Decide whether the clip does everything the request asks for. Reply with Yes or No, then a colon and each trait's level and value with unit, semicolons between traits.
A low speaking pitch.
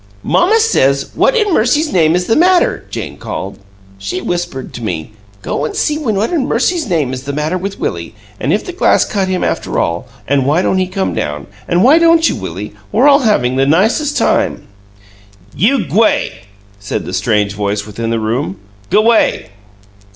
No: medium, 180 Hz